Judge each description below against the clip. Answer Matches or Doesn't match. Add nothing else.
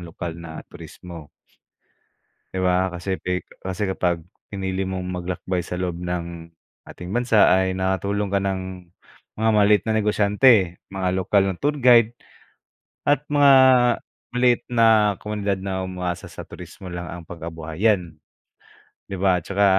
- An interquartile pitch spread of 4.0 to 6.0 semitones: Doesn't match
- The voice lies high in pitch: Doesn't match